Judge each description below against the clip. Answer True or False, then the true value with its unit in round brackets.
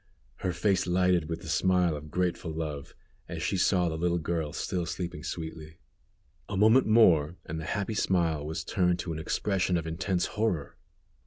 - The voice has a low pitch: True (85 Hz)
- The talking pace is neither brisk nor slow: True (175 wpm)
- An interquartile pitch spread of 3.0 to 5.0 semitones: False (2.6 semitones)